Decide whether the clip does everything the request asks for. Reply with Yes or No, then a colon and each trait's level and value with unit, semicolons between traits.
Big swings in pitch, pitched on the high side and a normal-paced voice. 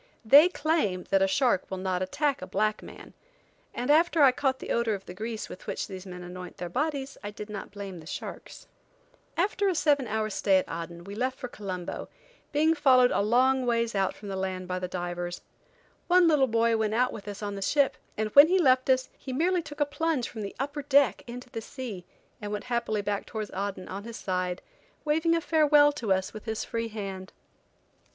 No: wide, 6.5 semitones; high, 225 Hz; fast, 215 wpm